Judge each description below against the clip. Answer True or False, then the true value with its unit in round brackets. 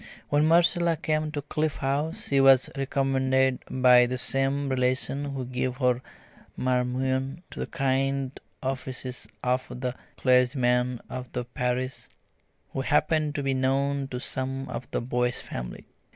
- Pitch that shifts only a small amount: True (1.7 semitones)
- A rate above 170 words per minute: False (140 wpm)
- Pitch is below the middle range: True (130 Hz)